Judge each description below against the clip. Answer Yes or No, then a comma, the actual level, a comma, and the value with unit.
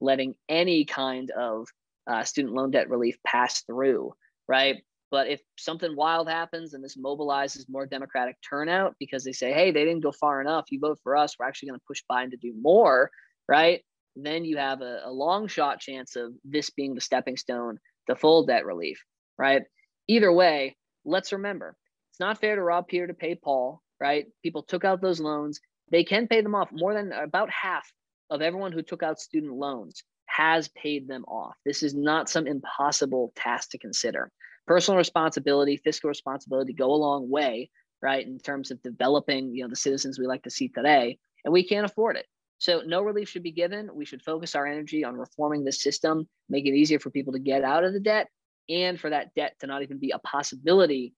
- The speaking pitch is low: No, medium, 145 Hz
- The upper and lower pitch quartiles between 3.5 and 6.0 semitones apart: Yes, average, 3.9 semitones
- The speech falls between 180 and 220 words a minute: Yes, fast, 205 wpm